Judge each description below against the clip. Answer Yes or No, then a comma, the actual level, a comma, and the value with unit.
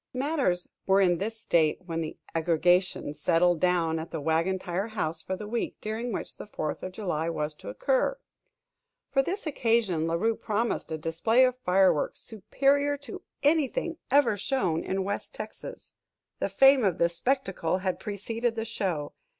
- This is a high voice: Yes, high, 195 Hz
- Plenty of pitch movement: Yes, wide, 5.9 semitones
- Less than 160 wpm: No, average, 165 wpm